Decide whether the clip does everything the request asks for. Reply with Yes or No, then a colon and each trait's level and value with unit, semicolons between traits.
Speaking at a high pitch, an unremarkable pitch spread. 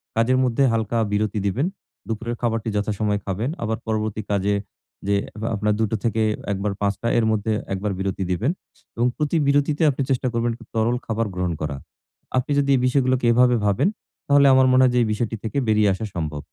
No: low, 110 Hz; average, 3.5 semitones